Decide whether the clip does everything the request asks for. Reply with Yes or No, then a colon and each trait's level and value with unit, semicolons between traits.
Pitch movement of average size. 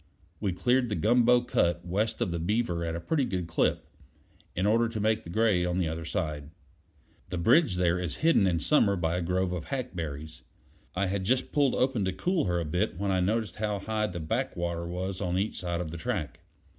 Yes: average, 4.3 semitones